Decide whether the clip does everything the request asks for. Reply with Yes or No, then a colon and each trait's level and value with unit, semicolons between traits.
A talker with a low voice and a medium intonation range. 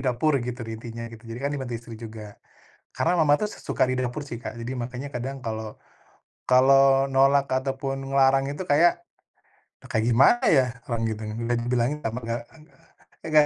Yes: low, 130 Hz; average, 3.0 semitones